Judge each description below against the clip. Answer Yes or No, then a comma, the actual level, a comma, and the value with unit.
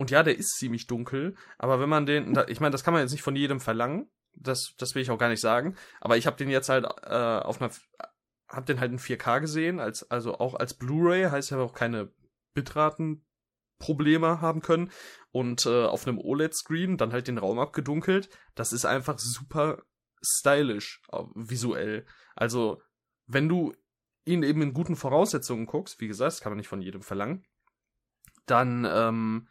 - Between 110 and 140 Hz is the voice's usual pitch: Yes, low, 135 Hz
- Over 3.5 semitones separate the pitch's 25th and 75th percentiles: Yes, average, 4.6 semitones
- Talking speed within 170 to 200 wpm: Yes, average, 185 wpm